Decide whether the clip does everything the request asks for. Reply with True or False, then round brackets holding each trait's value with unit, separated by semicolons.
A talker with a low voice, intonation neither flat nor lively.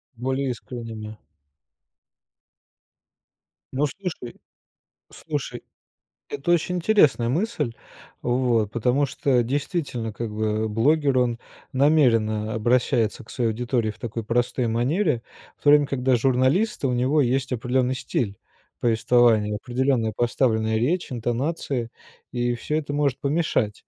True (125 Hz; 3.5 semitones)